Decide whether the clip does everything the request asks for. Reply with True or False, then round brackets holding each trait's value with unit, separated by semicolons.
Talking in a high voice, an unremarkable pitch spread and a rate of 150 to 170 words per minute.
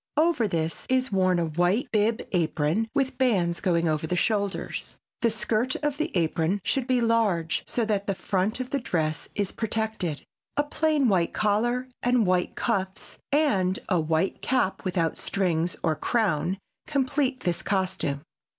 False (200 Hz; 6.0 semitones; 160 wpm)